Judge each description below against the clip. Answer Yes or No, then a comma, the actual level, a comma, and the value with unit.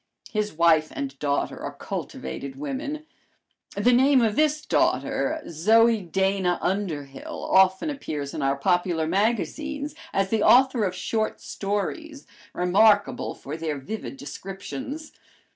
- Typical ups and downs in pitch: No, wide, 7.2 semitones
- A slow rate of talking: Yes, slow, 125 wpm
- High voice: Yes, high, 195 Hz